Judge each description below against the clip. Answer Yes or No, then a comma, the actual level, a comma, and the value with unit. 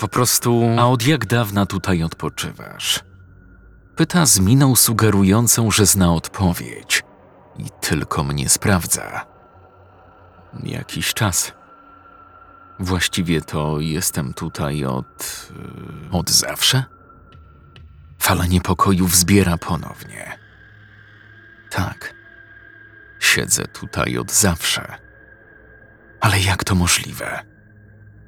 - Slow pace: Yes, slow, 90 wpm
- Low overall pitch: Yes, low, 100 Hz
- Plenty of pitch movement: No, average, 3.7 semitones